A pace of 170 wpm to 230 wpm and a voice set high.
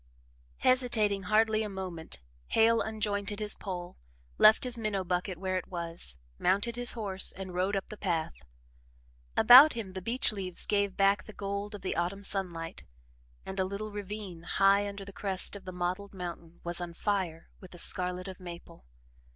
Yes: average, 175 wpm; high, 195 Hz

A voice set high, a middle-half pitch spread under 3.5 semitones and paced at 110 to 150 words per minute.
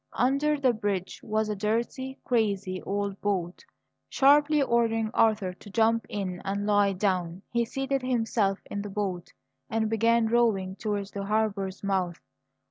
Yes: high, 210 Hz; average, 3.0 semitones; average, 145 wpm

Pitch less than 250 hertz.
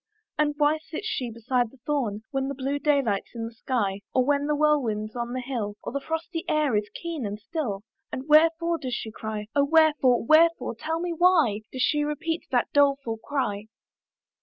No: very high, 275 Hz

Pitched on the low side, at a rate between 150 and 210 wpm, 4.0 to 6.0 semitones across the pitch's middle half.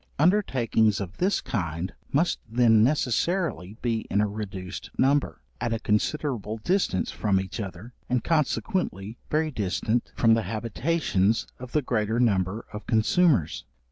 No: low, 115 Hz; average, 140 wpm; wide, 5.5 semitones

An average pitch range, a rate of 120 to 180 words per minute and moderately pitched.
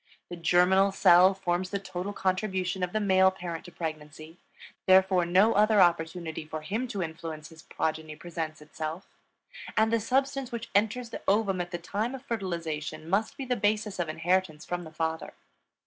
Yes: average, 3.9 semitones; average, 175 wpm; medium, 180 Hz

